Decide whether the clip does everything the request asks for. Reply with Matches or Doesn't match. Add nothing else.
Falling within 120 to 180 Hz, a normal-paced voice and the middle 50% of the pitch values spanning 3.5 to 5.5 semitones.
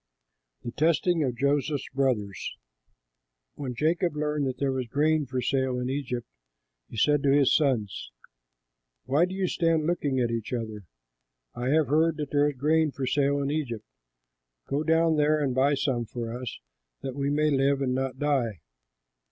Doesn't match